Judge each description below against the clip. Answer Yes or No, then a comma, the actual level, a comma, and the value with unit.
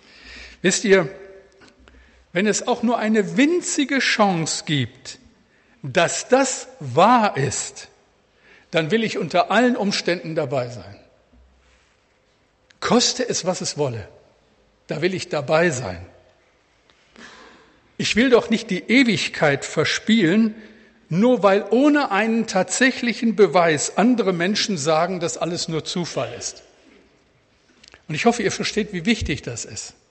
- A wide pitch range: Yes, wide, 5.9 semitones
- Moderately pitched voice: No, high, 195 Hz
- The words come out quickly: No, slow, 125 wpm